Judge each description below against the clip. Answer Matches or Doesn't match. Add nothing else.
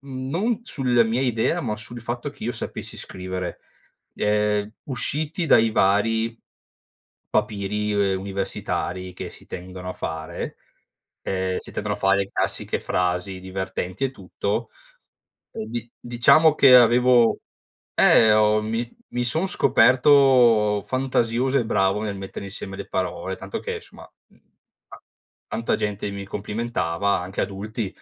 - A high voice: Doesn't match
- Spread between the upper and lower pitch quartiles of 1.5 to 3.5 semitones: Doesn't match